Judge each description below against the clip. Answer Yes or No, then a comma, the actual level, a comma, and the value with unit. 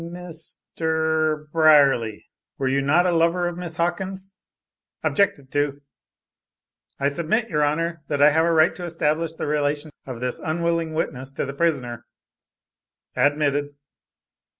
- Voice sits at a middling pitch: Yes, medium, 155 Hz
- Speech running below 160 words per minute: Yes, average, 140 wpm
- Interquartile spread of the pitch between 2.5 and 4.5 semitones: Yes, average, 2.8 semitones